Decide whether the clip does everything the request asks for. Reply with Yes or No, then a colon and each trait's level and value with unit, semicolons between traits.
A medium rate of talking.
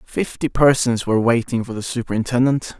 Yes: average, 150 wpm